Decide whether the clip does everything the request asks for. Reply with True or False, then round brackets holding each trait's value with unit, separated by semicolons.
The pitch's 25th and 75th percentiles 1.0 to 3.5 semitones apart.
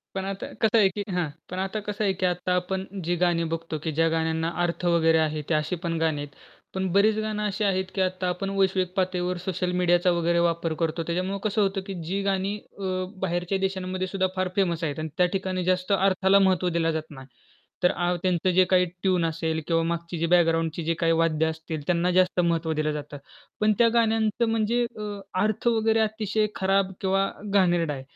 True (2.8 semitones)